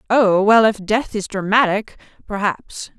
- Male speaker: No, female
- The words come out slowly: Yes, slow, 120 wpm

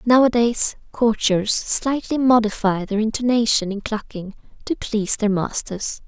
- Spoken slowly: Yes, slow, 120 wpm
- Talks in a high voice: Yes, high, 220 Hz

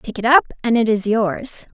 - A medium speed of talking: No, fast, 235 wpm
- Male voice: No, female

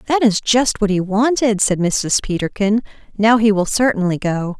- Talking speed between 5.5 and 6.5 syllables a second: No, 4.7 syllables/s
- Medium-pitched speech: No, high, 210 Hz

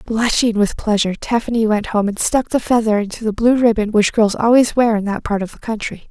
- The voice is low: No, high, 220 Hz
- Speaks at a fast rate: Yes, fast, 235 wpm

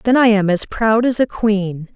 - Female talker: Yes, female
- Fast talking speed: Yes, fast, 245 wpm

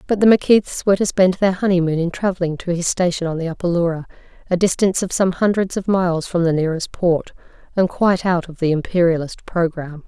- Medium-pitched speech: Yes, medium, 175 Hz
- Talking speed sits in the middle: No, fast, 210 wpm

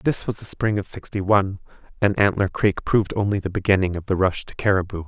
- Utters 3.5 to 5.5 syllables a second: No, 6.1 syllables/s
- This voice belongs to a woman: No, male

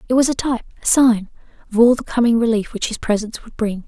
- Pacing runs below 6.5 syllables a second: No, 6.7 syllables/s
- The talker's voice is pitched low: No, high, 230 Hz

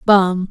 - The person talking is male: No, female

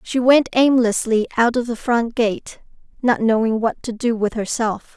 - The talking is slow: No, average, 180 wpm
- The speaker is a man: No, female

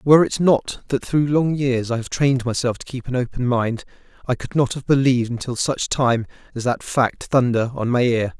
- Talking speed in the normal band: No, fast, 220 wpm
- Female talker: No, male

